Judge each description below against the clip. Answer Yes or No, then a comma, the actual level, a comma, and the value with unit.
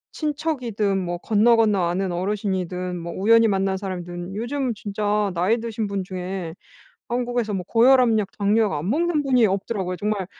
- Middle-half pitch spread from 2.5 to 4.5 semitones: Yes, average, 3.7 semitones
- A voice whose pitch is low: No, high, 205 Hz